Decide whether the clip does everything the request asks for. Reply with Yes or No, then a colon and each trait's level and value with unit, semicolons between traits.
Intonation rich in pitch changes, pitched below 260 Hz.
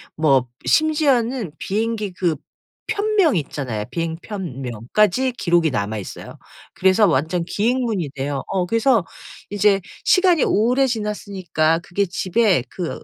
Yes: wide, 6.4 semitones; high, 190 Hz